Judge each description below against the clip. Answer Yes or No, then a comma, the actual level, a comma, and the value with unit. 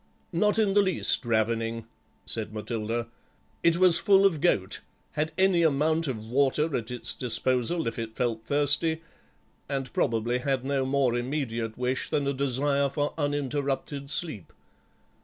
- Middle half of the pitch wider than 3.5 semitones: Yes, average, 4.8 semitones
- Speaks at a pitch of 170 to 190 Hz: No, low, 135 Hz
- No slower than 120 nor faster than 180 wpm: Yes, average, 145 wpm